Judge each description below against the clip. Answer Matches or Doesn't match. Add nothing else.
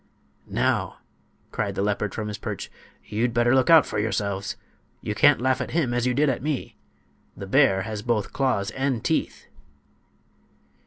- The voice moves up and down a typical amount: Matches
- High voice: Doesn't match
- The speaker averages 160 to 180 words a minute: Matches